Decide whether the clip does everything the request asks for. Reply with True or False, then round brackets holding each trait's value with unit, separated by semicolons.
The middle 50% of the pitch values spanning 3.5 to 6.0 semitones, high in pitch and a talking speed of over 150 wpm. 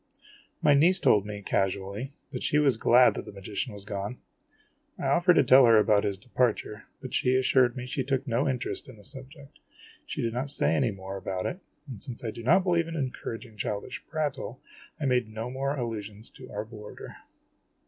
False (4.4 semitones; 120 Hz; 200 wpm)